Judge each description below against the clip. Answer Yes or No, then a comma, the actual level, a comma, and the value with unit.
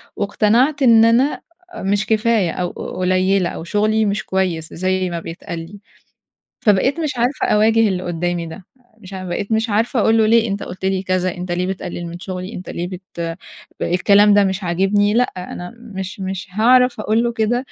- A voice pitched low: No, high, 195 Hz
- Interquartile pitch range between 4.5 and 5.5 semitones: No, average, 3.4 semitones